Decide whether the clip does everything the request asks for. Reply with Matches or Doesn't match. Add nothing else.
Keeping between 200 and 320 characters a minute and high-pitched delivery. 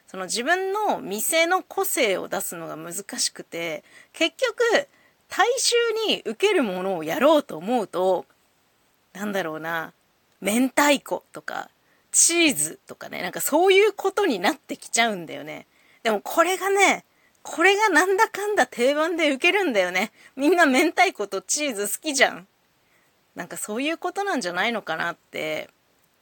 Matches